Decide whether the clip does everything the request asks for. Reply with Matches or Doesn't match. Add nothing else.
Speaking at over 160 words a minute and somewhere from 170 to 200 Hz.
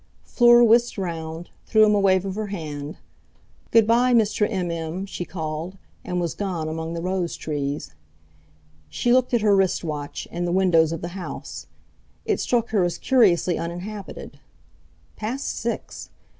Doesn't match